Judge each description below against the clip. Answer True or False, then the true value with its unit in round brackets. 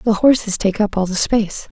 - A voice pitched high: True (210 Hz)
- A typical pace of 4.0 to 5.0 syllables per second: False (5.7 syllables/s)